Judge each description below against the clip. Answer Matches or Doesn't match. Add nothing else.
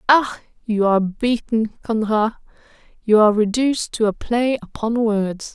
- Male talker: Doesn't match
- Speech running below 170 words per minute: Matches